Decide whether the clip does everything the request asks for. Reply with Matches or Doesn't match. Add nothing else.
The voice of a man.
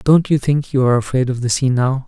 Matches